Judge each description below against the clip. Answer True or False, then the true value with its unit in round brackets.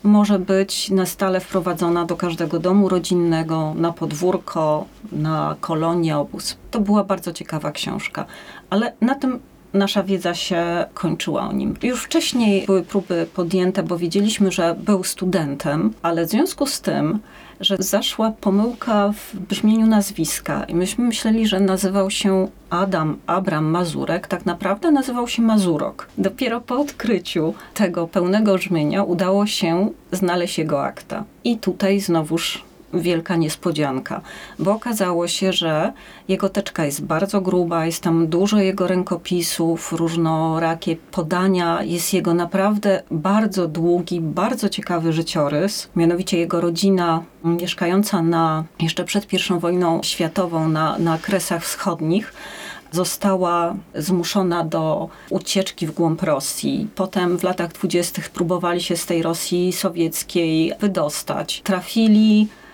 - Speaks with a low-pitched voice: False (180 Hz)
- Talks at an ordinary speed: True (130 wpm)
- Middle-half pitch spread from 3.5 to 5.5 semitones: False (2.8 semitones)